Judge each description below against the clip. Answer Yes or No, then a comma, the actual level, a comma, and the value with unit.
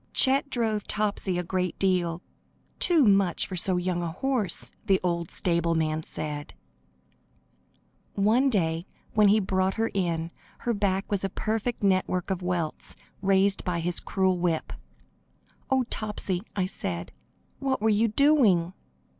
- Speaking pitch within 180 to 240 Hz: Yes, high, 190 Hz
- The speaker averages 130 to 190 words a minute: Yes, average, 140 wpm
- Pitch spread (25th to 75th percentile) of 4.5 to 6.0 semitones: No, average, 3.5 semitones